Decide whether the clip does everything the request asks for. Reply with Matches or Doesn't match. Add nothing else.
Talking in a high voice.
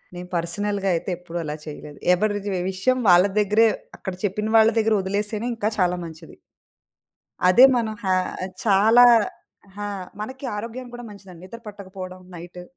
Matches